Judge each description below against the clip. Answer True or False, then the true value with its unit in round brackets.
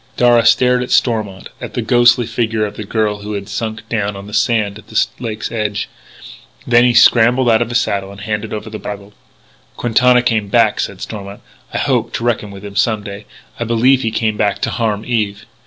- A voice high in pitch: False (110 Hz)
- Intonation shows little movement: True (2.3 semitones)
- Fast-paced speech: True (210 wpm)